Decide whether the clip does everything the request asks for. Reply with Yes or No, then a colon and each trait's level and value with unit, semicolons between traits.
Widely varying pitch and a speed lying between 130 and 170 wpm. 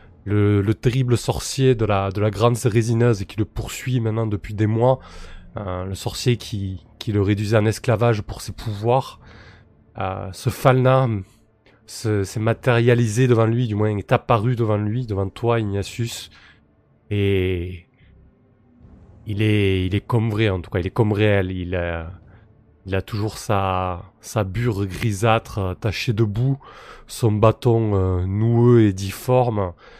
No: average, 3.2 semitones; average, 160 wpm